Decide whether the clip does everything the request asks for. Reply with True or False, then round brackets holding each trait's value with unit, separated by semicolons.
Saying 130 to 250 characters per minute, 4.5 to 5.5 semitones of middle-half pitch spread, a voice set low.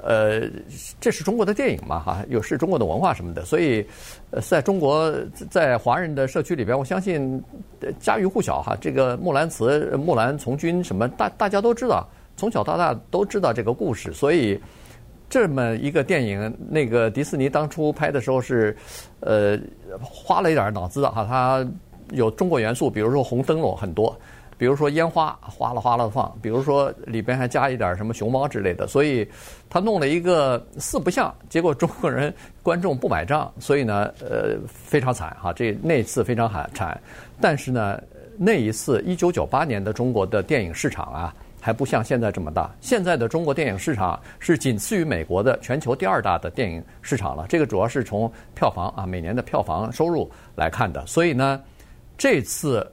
False (285 characters per minute; 5.1 semitones; 130 Hz)